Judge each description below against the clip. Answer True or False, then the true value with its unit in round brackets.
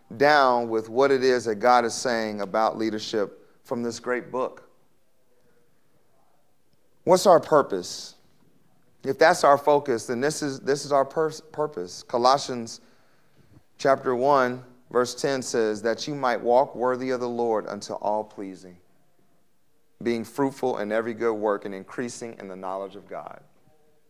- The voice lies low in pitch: True (125 Hz)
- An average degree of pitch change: True (3.8 semitones)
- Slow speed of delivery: False (150 wpm)